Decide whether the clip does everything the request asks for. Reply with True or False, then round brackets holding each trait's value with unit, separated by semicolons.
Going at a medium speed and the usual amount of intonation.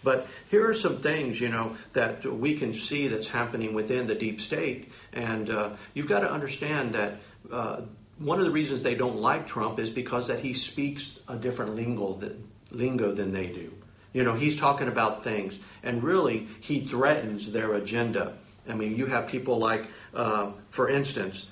True (185 wpm; 3.6 semitones)